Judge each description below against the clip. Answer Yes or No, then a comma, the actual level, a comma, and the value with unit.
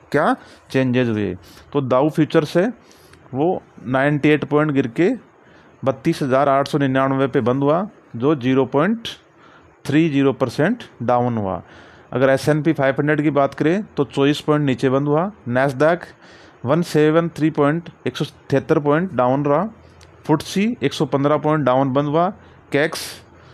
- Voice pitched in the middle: Yes, medium, 145 Hz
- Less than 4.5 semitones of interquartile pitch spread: Yes, average, 2.8 semitones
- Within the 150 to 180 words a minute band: Yes, average, 165 wpm